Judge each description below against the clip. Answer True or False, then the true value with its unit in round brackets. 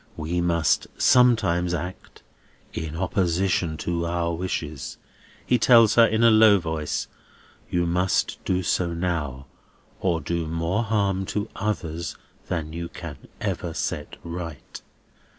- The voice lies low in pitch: True (85 Hz)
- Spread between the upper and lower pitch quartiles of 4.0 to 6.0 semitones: False (2.8 semitones)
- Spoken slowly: True (130 wpm)